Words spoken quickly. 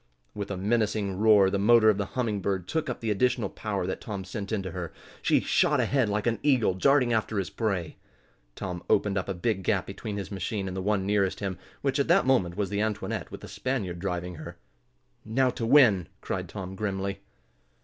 Yes: fast, 210 wpm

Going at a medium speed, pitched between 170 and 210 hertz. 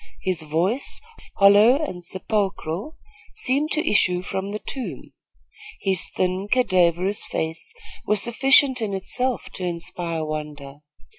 No: slow, 120 wpm; high, 190 Hz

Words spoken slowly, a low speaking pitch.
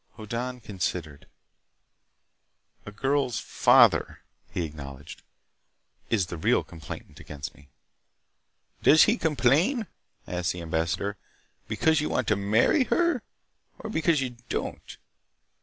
Yes: slow, 110 wpm; low, 110 Hz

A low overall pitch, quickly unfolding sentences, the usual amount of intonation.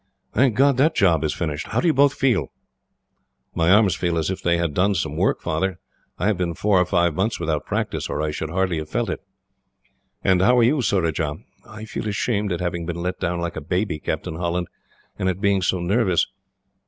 Yes: very low, 90 Hz; fast, 215 wpm; average, 3.6 semitones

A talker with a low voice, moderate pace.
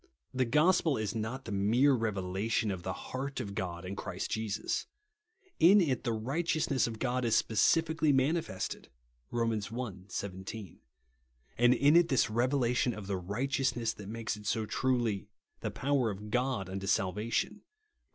Yes: low, 115 Hz; average, 170 wpm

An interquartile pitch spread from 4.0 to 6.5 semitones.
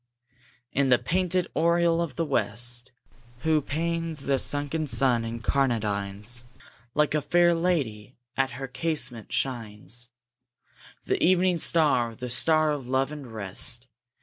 Yes: average, 5.2 semitones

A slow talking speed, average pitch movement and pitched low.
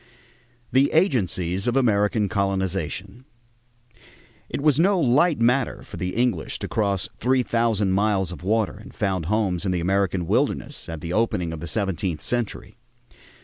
No: average, 150 wpm; average, 4.5 semitones; low, 100 Hz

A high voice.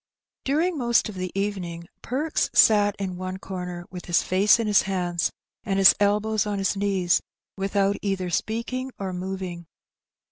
Yes: high, 195 Hz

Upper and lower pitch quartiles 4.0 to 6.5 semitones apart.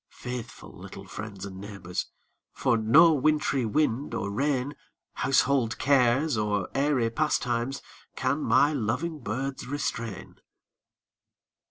Yes: average, 4.6 semitones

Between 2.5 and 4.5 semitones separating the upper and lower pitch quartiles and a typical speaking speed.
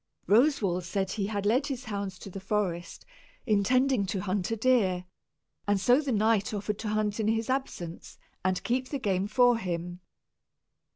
Yes: average, 3.9 semitones; average, 170 wpm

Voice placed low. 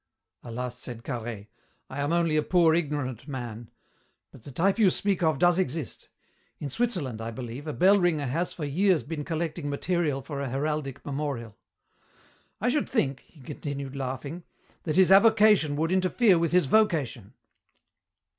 No: medium, 150 Hz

